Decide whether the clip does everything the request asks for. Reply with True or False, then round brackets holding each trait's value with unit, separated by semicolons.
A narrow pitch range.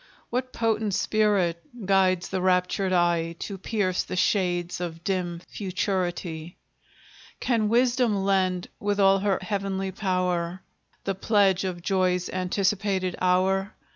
True (1.9 semitones)